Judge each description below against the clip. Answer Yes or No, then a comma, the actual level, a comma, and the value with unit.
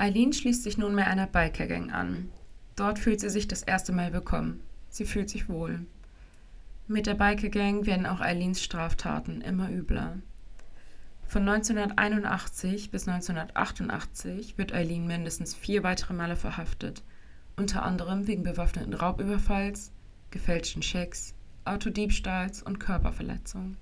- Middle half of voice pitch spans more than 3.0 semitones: Yes, average, 3.8 semitones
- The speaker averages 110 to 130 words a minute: Yes, slow, 125 wpm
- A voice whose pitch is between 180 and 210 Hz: Yes, medium, 185 Hz